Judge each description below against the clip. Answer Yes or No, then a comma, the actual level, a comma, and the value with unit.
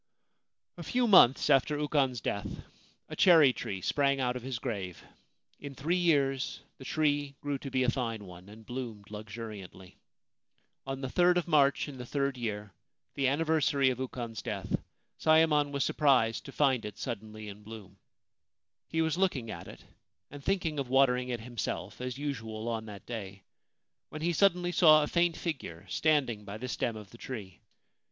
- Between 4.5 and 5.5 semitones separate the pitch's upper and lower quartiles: Yes, average, 5.0 semitones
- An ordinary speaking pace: Yes, average, 175 wpm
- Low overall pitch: Yes, low, 130 Hz